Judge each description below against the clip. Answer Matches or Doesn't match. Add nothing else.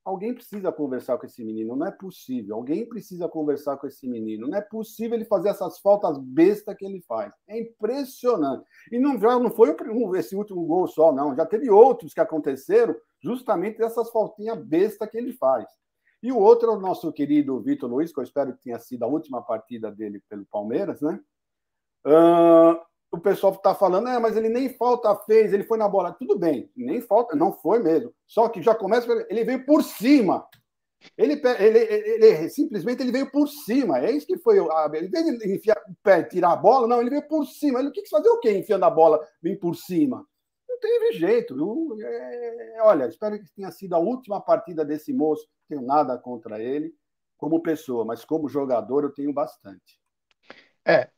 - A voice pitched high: Matches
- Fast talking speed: Matches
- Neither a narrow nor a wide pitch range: Doesn't match